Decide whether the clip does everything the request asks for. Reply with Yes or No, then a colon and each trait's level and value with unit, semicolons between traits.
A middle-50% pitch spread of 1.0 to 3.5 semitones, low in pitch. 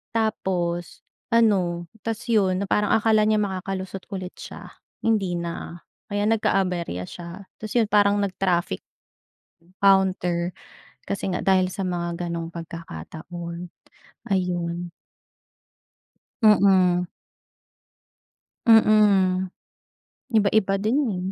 No: average, 2.9 semitones; medium, 185 Hz